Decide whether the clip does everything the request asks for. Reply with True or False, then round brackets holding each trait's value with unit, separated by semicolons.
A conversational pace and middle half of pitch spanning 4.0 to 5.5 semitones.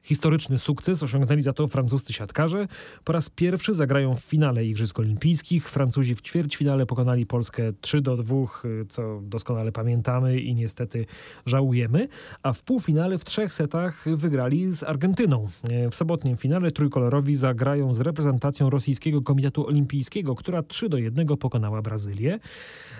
True (140 wpm; 4.3 semitones)